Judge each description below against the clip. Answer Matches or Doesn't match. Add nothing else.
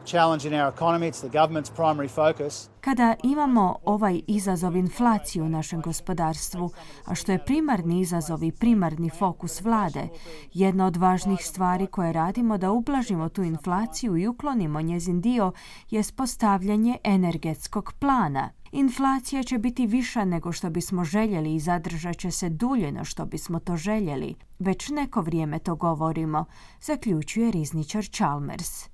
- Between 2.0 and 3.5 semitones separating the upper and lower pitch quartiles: Doesn't match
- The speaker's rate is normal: Matches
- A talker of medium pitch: Matches